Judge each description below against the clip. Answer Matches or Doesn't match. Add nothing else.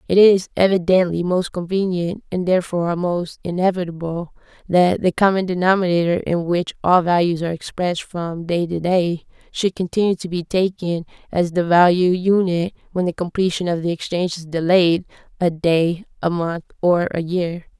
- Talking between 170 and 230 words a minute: Doesn't match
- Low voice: Doesn't match